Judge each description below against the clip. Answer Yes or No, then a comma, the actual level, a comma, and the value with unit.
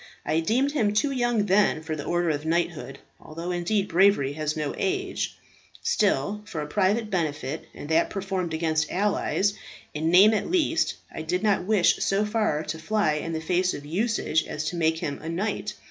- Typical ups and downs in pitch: Yes, average, 4.8 semitones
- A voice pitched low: No, medium, 175 Hz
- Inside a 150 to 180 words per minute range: No, average, 190 wpm